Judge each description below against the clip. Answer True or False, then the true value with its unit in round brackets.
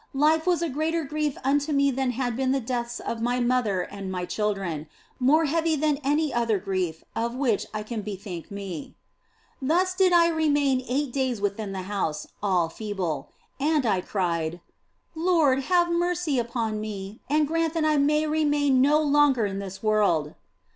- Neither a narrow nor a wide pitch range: False (7.0 semitones)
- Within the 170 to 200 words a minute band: True (175 wpm)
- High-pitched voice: True (255 Hz)